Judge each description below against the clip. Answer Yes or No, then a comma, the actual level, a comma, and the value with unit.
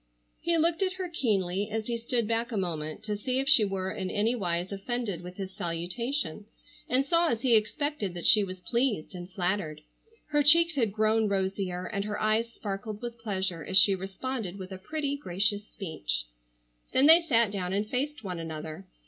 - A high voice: Yes, high, 210 Hz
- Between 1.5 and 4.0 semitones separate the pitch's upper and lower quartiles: No, average, 4.8 semitones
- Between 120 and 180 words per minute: No, average, 190 wpm